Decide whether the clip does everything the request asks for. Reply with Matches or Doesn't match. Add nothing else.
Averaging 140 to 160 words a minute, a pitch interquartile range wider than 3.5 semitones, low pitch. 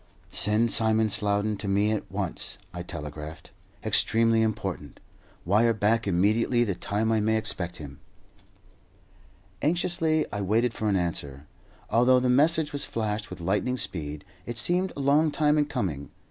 Matches